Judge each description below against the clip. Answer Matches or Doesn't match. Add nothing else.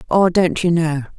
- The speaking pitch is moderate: Matches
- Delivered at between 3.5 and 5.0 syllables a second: Matches